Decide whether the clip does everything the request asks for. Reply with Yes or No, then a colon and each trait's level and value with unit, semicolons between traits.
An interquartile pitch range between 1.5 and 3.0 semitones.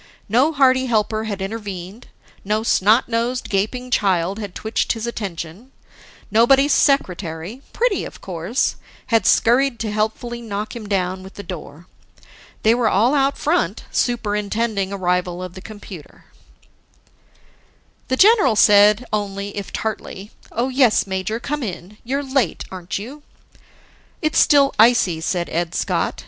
No: average, 4.3 semitones